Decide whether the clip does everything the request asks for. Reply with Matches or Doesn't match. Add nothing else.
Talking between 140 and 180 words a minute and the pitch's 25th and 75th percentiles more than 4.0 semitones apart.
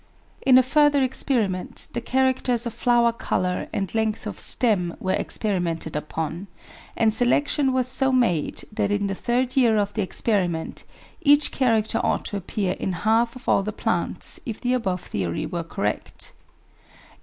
Matches